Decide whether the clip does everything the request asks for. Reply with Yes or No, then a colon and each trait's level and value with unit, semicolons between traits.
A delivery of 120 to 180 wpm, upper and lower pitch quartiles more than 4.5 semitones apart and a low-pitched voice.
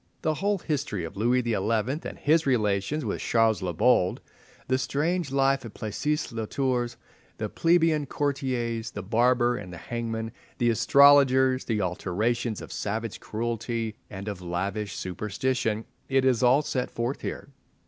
No: average, 150 wpm; average, 4.1 semitones; low, 120 Hz